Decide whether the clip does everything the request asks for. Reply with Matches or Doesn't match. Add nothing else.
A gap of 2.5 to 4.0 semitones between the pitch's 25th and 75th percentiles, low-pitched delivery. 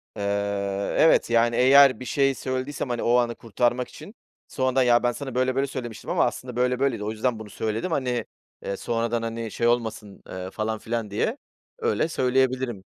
Matches